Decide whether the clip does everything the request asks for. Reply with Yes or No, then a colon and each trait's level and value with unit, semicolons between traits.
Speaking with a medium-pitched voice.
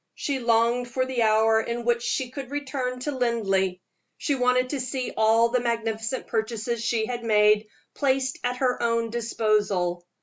No: high, 235 Hz